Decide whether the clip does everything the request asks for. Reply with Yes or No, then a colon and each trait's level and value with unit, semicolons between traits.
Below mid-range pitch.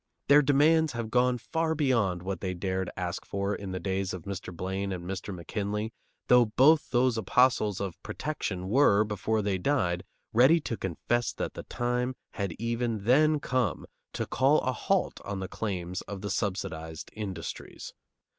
Yes: low, 105 Hz